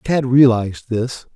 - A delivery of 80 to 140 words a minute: Yes, slow, 135 wpm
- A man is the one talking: Yes, male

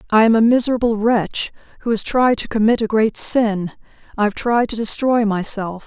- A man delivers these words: No, female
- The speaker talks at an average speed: Yes, average, 185 wpm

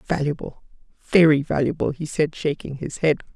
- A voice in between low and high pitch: Yes, medium, 150 Hz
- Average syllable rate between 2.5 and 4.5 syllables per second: No, 5.0 syllables/s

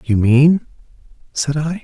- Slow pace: Yes, slow, 130 wpm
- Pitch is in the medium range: Yes, medium, 145 Hz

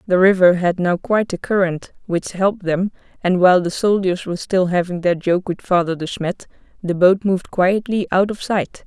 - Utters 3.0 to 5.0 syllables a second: No, 5.2 syllables/s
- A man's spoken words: No, female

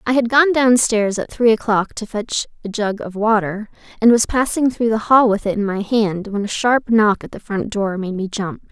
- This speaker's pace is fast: Yes, fast, 250 wpm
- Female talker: Yes, female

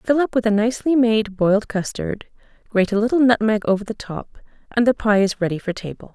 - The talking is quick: Yes, fast, 215 wpm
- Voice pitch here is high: Yes, high, 215 Hz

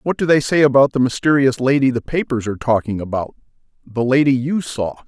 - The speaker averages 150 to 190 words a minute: No, average, 200 wpm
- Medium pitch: No, low, 130 Hz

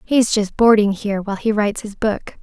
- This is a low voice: No, high, 210 Hz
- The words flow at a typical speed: No, fast, 220 wpm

